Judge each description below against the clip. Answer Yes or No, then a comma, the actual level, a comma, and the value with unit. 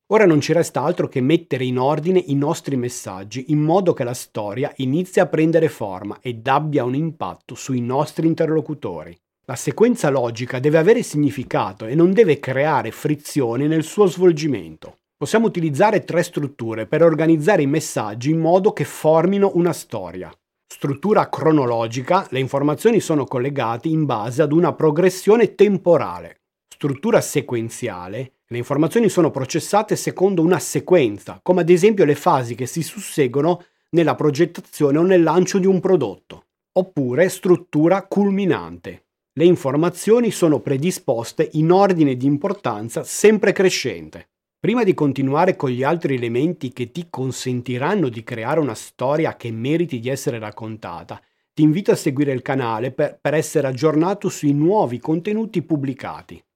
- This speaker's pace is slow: No, average, 145 wpm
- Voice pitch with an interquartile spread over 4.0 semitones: Yes, average, 5.1 semitones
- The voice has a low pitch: No, medium, 155 Hz